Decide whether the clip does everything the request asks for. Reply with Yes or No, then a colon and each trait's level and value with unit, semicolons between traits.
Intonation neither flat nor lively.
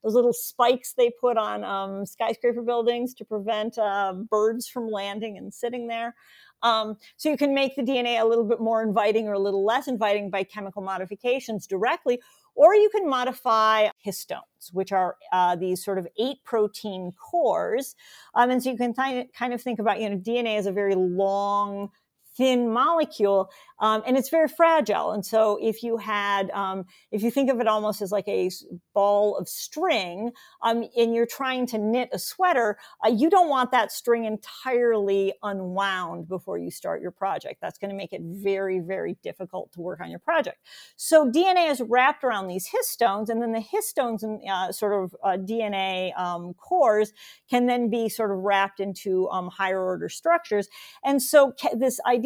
Yes: average, 4.0 semitones